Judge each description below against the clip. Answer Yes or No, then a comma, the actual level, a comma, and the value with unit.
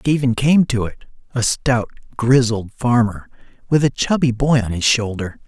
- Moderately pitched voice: No, low, 120 Hz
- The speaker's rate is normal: Yes, average, 165 wpm